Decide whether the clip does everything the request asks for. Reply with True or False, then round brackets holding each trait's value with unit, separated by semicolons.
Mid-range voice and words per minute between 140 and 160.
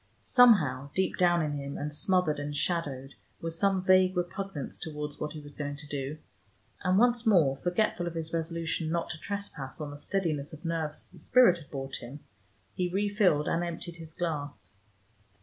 False (165 Hz; 175 wpm)